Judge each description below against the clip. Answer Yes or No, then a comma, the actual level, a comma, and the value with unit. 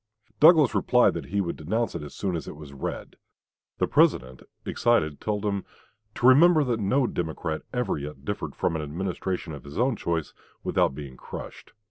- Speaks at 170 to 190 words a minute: Yes, average, 180 wpm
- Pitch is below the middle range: Yes, very low, 90 Hz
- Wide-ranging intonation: Yes, wide, 7.8 semitones